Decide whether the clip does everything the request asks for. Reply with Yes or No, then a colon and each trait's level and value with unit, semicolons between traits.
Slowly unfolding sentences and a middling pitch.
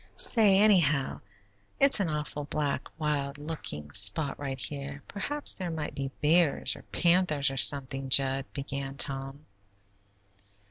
Yes: slow, 130 wpm; medium, 145 Hz